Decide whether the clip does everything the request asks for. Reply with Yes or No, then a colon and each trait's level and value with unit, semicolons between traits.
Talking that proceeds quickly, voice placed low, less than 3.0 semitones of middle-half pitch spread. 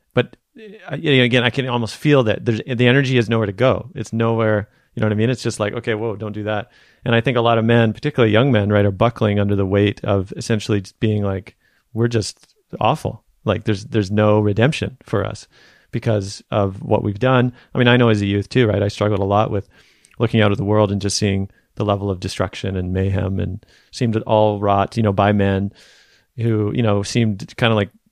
Yes: fast, 230 wpm; low, 110 Hz; narrow, 2.6 semitones